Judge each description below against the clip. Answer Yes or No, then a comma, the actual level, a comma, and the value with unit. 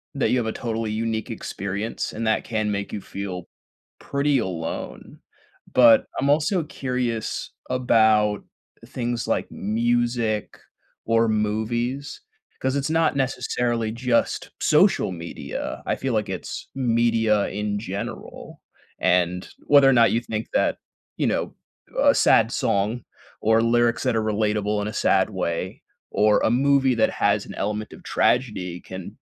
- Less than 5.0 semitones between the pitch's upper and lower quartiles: Yes, average, 2.8 semitones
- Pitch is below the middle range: Yes, low, 115 Hz